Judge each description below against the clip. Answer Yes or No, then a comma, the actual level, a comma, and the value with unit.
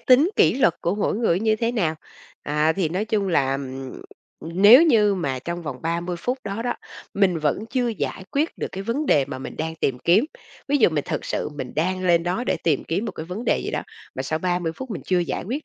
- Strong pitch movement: Yes, wide, 5.8 semitones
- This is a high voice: No, medium, 180 Hz